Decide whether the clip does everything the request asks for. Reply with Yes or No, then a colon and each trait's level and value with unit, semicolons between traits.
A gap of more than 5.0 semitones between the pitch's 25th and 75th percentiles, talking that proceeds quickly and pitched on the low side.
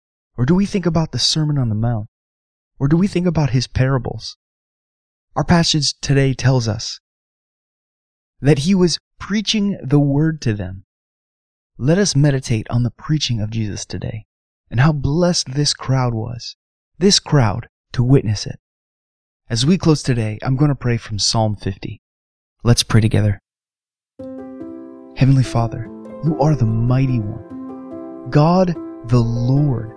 No: wide, 5.6 semitones; average, 150 wpm; low, 125 Hz